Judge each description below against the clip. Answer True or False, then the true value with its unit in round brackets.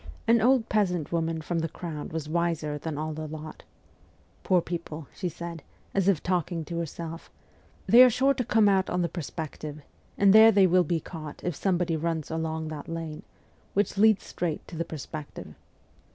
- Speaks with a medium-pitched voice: True (170 Hz)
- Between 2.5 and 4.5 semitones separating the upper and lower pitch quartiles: True (3.1 semitones)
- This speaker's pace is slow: False (190 wpm)